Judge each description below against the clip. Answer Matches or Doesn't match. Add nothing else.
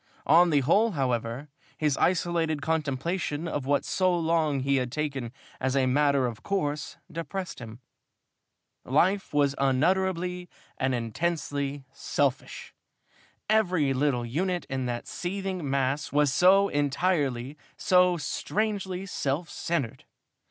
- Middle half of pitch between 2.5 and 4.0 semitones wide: Doesn't match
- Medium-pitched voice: Matches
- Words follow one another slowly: Matches